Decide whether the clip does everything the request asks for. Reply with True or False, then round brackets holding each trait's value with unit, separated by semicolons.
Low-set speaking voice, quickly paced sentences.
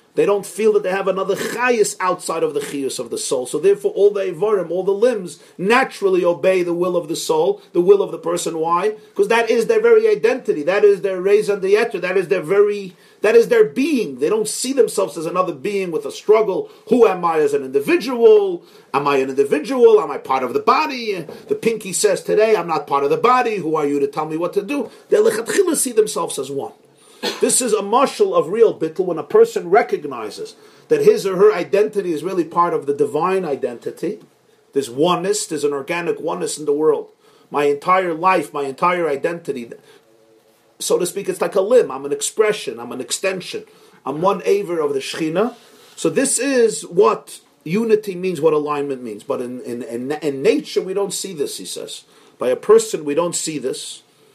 False (240 Hz; 210 wpm)